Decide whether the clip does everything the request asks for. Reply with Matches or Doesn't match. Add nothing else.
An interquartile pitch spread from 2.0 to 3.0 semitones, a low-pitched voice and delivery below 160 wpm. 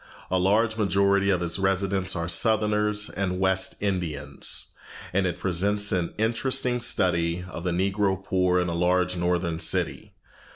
Matches